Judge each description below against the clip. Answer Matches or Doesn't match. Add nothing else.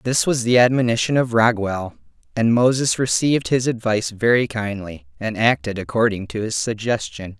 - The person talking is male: Matches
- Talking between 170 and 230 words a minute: Doesn't match